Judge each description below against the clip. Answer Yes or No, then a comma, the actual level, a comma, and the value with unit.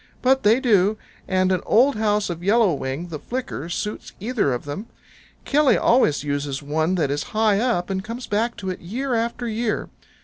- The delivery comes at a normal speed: Yes, average, 190 wpm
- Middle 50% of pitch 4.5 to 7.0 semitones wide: Yes, wide, 5.6 semitones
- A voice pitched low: No, high, 205 Hz